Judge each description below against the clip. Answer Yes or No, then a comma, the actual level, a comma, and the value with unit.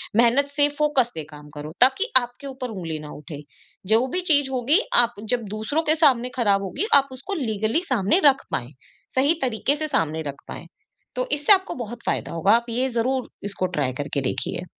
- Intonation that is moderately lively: No, wide, 6.2 semitones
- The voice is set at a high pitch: Yes, high, 240 Hz